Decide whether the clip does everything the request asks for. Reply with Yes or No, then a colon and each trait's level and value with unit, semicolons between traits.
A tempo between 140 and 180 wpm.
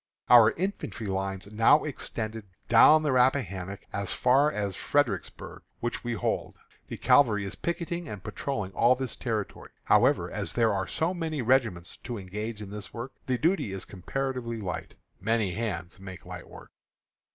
Yes: average, 160 wpm